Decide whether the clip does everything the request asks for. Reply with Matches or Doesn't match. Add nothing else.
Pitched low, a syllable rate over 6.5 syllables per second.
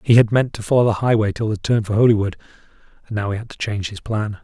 Matches